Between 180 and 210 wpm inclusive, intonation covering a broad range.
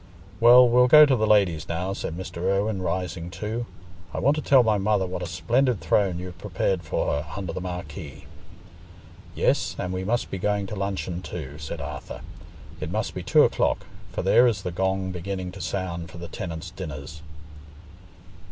No: average, 185 wpm; average, 3.3 semitones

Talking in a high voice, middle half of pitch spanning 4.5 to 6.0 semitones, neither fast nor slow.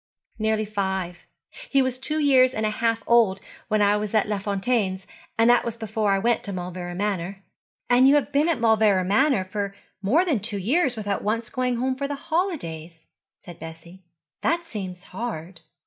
Yes: high, 215 Hz; average, 4.8 semitones; average, 180 wpm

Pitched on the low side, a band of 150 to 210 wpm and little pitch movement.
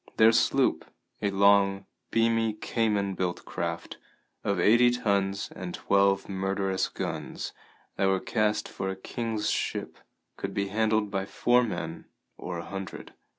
No: low, 100 Hz; average, 140 wpm; narrow, 2.2 semitones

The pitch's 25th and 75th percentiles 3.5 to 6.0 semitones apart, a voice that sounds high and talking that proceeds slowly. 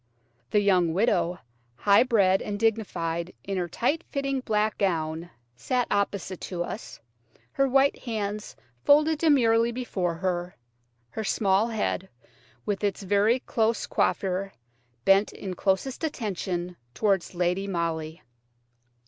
Yes: average, 4.1 semitones; high, 200 Hz; slow, 125 wpm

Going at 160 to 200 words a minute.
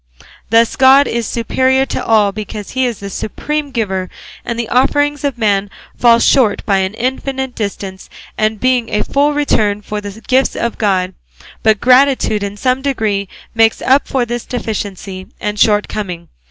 Yes: average, 165 wpm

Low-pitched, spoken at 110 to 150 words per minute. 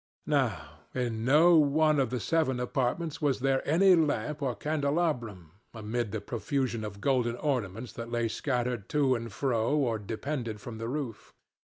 No: low, 125 Hz; average, 160 wpm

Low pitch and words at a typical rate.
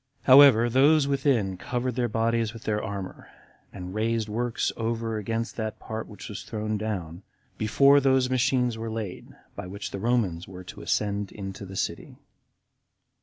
Yes: low, 110 Hz; average, 160 wpm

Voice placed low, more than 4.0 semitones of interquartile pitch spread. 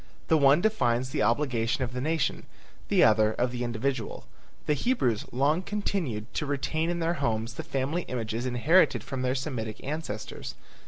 Yes: low, 130 Hz; average, 4.9 semitones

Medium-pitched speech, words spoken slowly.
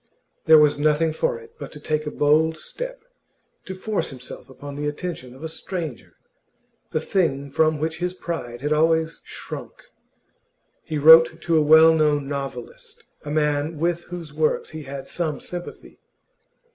No: medium, 155 Hz; average, 160 wpm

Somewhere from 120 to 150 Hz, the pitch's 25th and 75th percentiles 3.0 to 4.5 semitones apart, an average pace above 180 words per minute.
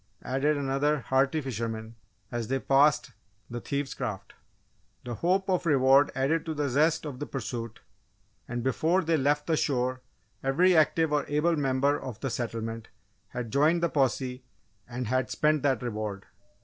No: low, 135 Hz; average, 3.4 semitones; average, 160 wpm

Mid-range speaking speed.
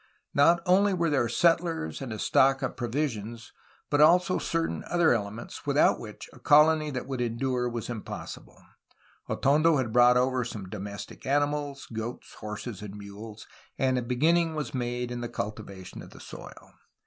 Yes: average, 160 wpm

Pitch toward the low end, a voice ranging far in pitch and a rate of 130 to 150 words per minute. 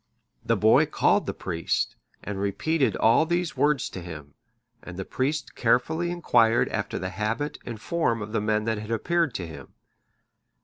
No: low, 115 Hz; wide, 7.1 semitones; average, 170 wpm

